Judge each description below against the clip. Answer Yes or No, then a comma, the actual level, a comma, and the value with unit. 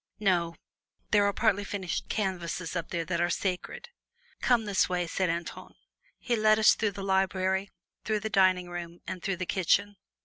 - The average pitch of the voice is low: No, high, 190 Hz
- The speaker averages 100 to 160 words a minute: No, average, 180 wpm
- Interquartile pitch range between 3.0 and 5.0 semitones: No, narrow, 2.6 semitones